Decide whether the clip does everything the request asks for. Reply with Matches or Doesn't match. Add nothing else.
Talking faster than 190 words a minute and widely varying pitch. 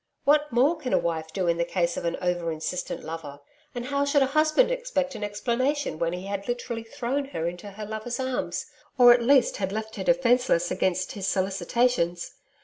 Matches